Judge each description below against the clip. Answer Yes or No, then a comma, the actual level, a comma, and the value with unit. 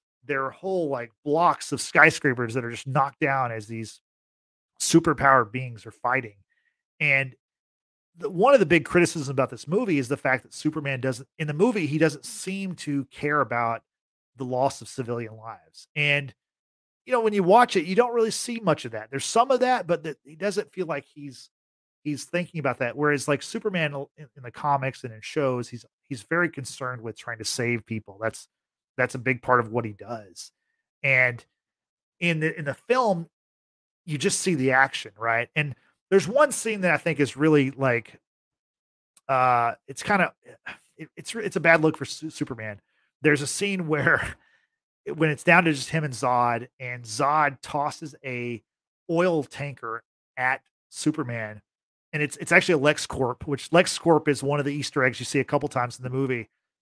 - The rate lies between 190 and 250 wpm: Yes, average, 195 wpm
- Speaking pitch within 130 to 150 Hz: Yes, medium, 140 Hz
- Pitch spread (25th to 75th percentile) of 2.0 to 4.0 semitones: No, average, 4.7 semitones